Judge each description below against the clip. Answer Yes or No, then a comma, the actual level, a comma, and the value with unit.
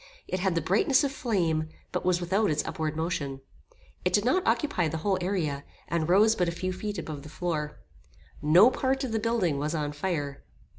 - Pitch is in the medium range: Yes, medium, 175 Hz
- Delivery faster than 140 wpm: Yes, average, 200 wpm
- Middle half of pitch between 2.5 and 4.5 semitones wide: No, average, 5.3 semitones